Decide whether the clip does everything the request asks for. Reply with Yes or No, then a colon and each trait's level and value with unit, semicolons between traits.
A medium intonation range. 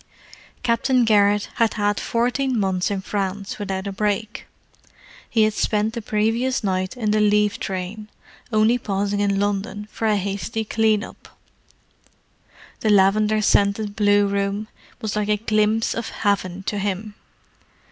No: narrow, 1.5 semitones